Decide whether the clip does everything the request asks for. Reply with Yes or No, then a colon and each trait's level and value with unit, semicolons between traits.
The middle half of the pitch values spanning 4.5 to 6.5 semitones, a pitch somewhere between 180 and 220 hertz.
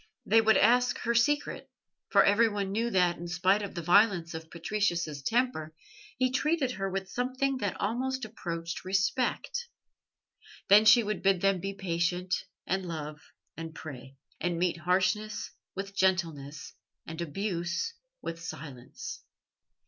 Yes: average, 4.8 semitones; high, 190 Hz